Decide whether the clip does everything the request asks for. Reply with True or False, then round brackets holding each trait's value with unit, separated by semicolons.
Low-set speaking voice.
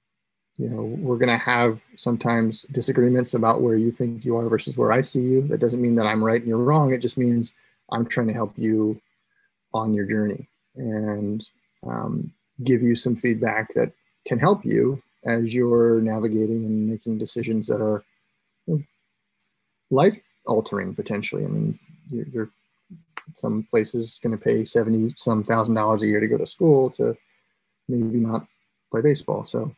True (115 Hz)